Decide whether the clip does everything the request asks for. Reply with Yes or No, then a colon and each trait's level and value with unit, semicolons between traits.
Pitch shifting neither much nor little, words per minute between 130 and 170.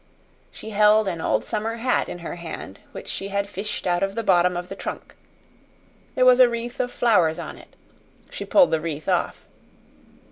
No: average, 4.8 semitones; average, 190 wpm